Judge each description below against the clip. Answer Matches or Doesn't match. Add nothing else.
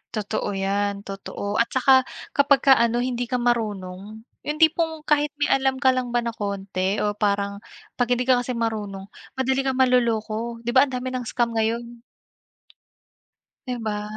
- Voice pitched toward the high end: Matches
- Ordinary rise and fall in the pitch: Matches